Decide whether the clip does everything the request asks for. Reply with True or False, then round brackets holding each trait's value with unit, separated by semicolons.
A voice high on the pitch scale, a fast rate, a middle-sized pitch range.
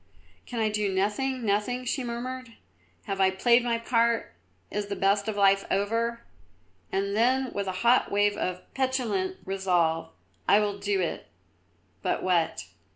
False (210 Hz; 155 wpm; 3.6 semitones)